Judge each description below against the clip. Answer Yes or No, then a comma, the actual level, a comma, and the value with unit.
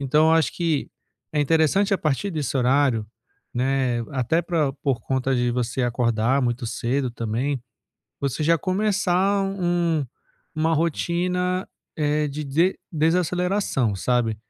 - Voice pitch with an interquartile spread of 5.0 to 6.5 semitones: Yes, wide, 5.4 semitones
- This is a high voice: No, medium, 150 Hz